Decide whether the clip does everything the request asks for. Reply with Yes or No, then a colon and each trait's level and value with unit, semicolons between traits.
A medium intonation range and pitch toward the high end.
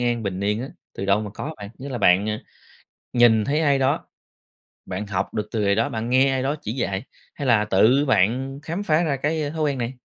No: average, 4.8 semitones; low, 120 Hz